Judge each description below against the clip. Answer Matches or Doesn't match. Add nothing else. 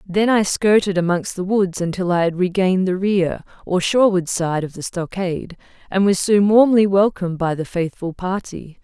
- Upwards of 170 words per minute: Matches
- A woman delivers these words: Matches